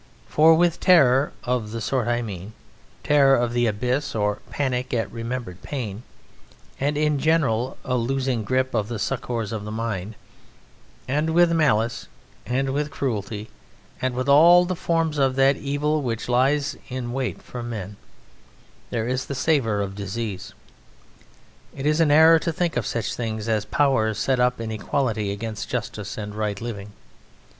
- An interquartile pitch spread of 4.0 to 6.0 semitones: Yes, average, 4.4 semitones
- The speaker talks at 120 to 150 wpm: No, average, 165 wpm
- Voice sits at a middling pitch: No, low, 125 Hz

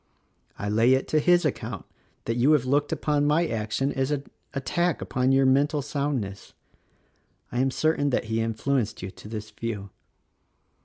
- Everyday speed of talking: Yes, average, 165 wpm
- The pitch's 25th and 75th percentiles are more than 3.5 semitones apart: Yes, average, 4.4 semitones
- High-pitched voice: No, low, 130 Hz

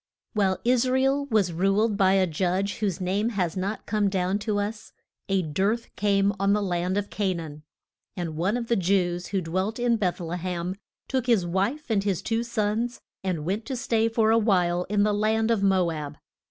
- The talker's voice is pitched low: No, high, 200 Hz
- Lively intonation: No, average, 3.4 semitones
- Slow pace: No, fast, 205 wpm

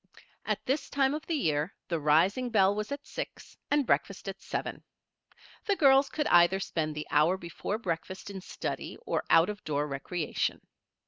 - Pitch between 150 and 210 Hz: Yes, high, 190 Hz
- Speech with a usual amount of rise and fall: No, wide, 8.0 semitones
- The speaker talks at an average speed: Yes, average, 175 wpm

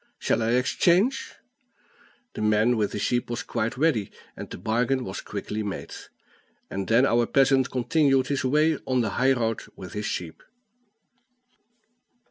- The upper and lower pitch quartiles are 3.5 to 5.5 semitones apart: Yes, average, 3.8 semitones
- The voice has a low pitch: Yes, low, 120 Hz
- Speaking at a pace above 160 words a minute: No, average, 150 wpm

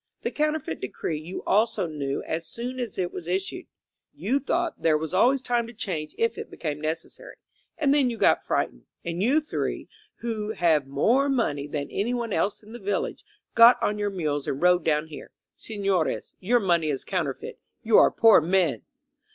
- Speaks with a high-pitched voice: Yes, high, 195 Hz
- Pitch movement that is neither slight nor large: No, wide, 6.9 semitones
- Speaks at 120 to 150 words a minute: No, average, 185 wpm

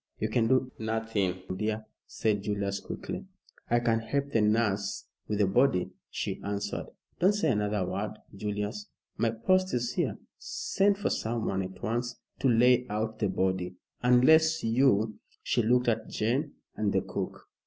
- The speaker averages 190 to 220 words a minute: No, average, 160 wpm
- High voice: No, low, 110 Hz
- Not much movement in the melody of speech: No, average, 3.3 semitones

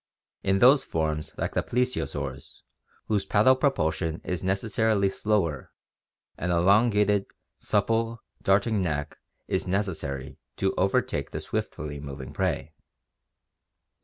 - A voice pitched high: No, very low, 95 Hz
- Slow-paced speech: Yes, slow, 110 wpm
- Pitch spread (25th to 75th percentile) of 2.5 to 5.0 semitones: No, wide, 5.6 semitones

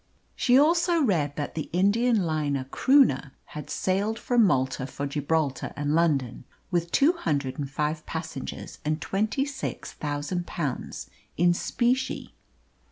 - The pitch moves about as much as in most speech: No, wide, 7.4 semitones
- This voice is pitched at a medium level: Yes, medium, 160 Hz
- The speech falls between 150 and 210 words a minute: No, slow, 135 wpm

